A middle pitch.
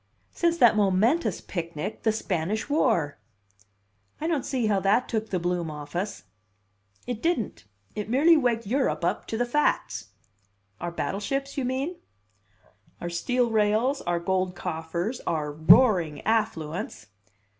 No: high, 215 Hz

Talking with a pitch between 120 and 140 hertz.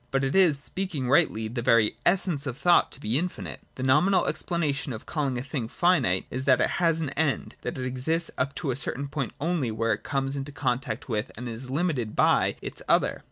Yes: low, 135 Hz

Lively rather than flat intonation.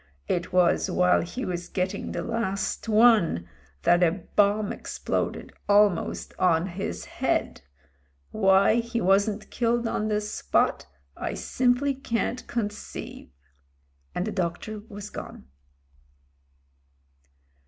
No: average, 4.0 semitones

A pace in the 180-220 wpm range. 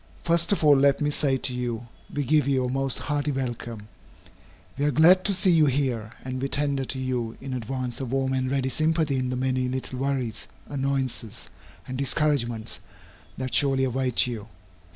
Yes: average, 185 wpm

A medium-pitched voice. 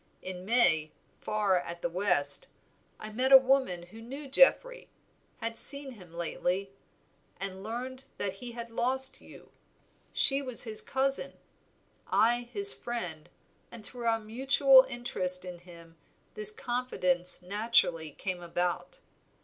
No: high, 220 Hz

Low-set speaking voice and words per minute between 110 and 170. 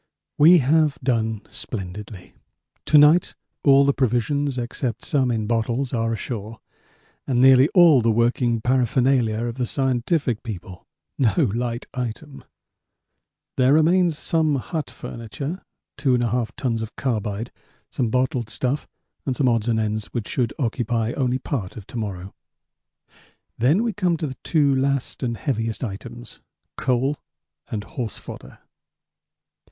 Yes: low, 125 Hz; slow, 135 wpm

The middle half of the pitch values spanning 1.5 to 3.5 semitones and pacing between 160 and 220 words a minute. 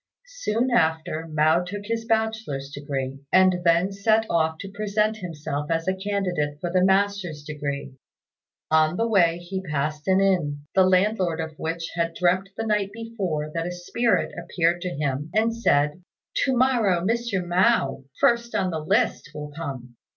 No: average, 4.9 semitones; average, 165 wpm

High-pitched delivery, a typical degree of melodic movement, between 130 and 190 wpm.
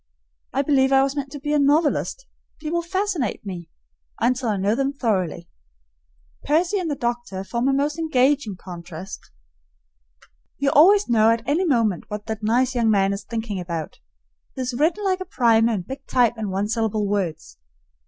No: high, 240 Hz; wide, 5.7 semitones; average, 175 wpm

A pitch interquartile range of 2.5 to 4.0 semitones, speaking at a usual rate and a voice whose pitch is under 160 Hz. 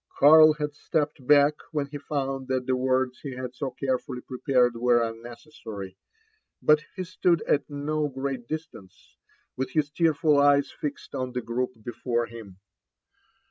Yes: average, 3.1 semitones; average, 150 wpm; low, 135 Hz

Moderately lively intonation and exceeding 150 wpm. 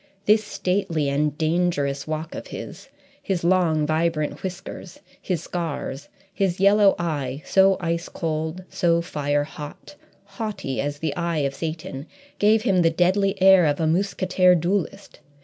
No: average, 3.7 semitones; average, 145 wpm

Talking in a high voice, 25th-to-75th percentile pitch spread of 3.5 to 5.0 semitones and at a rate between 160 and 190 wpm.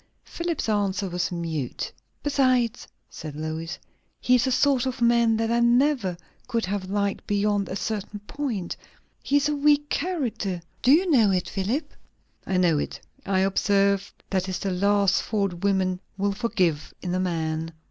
Yes: high, 200 Hz; average, 4.7 semitones; average, 165 wpm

